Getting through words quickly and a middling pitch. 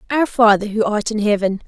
No: fast, 215 wpm; high, 215 Hz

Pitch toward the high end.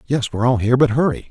No: low, 125 Hz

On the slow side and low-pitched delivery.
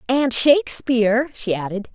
No: slow, 125 wpm; high, 240 Hz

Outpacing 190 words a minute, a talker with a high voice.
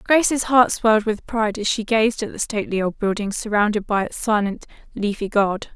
Yes: average, 200 wpm; high, 215 Hz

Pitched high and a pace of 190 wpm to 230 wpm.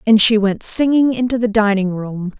Yes: high, 215 Hz; average, 200 wpm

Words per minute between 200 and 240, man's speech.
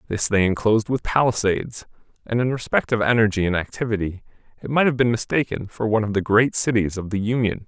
Yes: fast, 205 wpm; male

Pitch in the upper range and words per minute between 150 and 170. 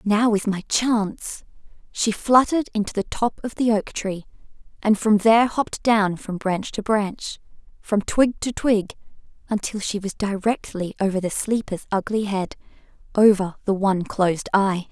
Yes: high, 205 Hz; average, 160 wpm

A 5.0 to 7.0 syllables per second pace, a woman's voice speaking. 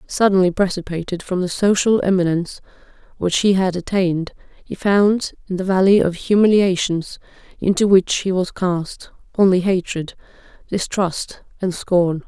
No: 4.7 syllables/s; female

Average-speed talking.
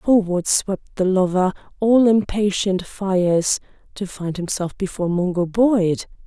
No: slow, 115 wpm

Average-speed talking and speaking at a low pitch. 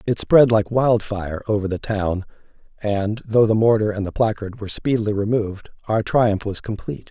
Yes: average, 175 wpm; low, 105 Hz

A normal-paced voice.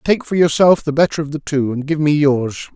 No: fast, 260 wpm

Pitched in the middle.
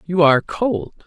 Yes: medium, 170 Hz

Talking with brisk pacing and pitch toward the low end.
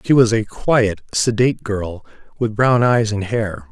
No: average, 180 wpm; low, 110 Hz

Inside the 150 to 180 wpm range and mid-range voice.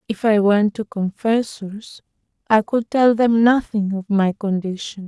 No: average, 155 wpm; high, 210 Hz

